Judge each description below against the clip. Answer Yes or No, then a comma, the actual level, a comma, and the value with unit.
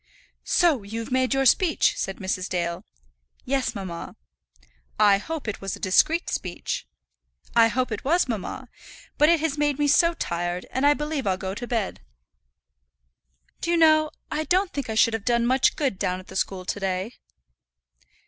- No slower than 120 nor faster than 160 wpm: No, average, 175 wpm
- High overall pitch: Yes, high, 240 Hz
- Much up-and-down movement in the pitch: Yes, wide, 7.3 semitones